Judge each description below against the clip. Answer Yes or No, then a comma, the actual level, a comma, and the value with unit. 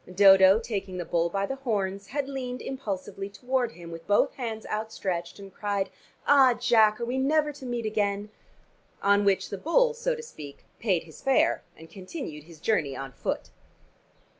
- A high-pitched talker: Yes, high, 205 Hz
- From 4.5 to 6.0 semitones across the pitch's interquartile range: Yes, average, 5.2 semitones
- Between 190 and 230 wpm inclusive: No, average, 175 wpm